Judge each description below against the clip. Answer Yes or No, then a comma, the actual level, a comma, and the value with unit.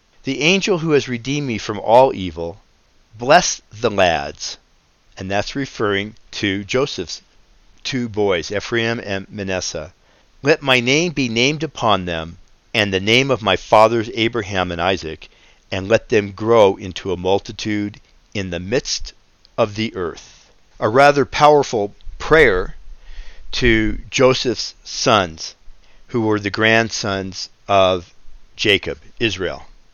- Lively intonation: No, average, 4.6 semitones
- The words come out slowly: Yes, slow, 130 wpm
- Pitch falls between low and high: No, low, 110 Hz